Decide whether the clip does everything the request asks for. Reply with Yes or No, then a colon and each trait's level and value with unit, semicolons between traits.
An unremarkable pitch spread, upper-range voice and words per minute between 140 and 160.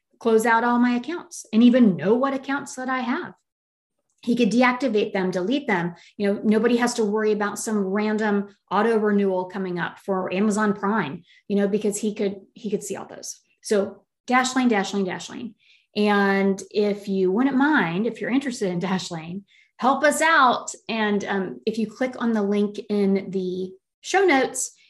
No: average, 3.4 semitones; high, 210 Hz; average, 180 wpm